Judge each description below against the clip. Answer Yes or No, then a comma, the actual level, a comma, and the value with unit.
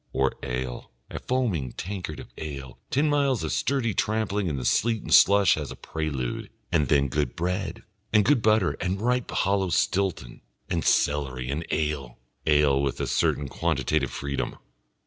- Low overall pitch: Yes, very low, 80 Hz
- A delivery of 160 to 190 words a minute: Yes, average, 165 wpm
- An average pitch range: No, wide, 7.0 semitones